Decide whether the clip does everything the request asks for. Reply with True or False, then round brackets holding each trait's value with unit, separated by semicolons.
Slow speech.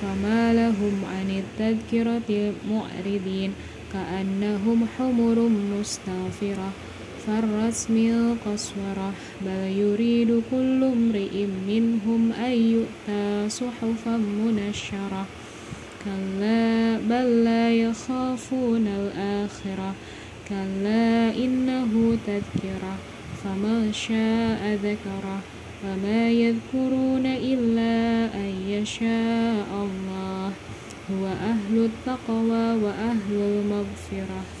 True (70 wpm)